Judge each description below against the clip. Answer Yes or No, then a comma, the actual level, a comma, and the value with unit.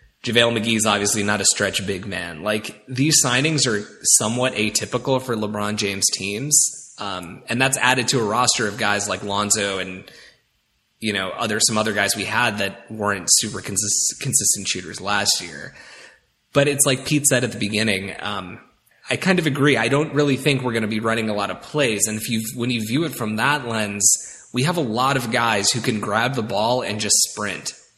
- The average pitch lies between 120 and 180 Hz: No, low, 110 Hz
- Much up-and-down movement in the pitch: No, average, 3.7 semitones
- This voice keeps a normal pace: No, fast, 210 wpm